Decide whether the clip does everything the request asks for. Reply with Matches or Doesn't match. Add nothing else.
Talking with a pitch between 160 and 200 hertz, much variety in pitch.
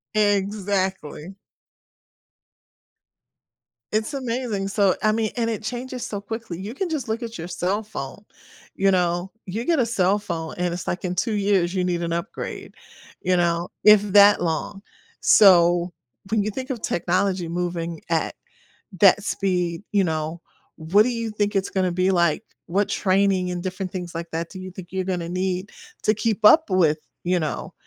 Doesn't match